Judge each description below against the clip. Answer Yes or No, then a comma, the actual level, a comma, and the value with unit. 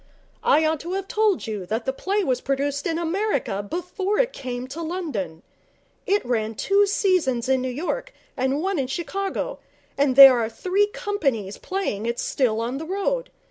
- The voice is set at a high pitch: Yes, very high, 300 Hz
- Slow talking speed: No, average, 180 wpm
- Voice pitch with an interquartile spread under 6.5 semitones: No, wide, 7.8 semitones